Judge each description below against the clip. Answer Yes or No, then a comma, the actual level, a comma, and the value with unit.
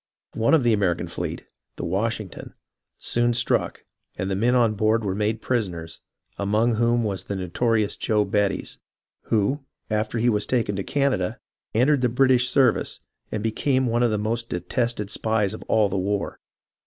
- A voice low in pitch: Yes, low, 110 Hz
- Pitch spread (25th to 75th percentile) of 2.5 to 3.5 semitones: Yes, average, 2.9 semitones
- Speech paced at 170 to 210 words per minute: Yes, average, 175 wpm